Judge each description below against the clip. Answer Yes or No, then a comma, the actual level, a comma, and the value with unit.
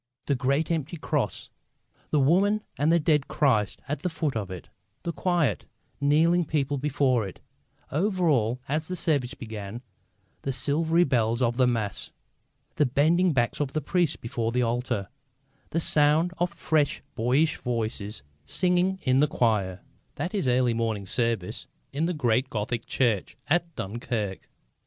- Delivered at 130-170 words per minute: Yes, average, 155 wpm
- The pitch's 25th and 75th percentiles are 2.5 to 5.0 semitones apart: No, wide, 5.5 semitones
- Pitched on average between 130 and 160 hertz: Yes, medium, 140 Hz